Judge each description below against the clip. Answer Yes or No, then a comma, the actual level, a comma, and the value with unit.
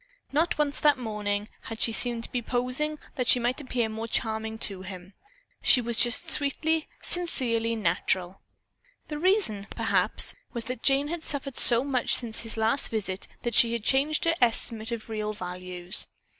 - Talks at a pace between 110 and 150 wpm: No, average, 170 wpm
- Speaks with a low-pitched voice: No, high, 235 Hz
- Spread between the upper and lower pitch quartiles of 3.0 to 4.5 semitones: Yes, average, 4.1 semitones